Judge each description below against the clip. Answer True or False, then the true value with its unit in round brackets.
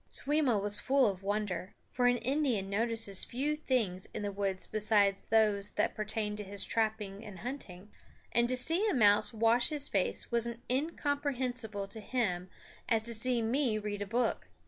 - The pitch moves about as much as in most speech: True (3.7 semitones)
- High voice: True (220 Hz)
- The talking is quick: False (175 wpm)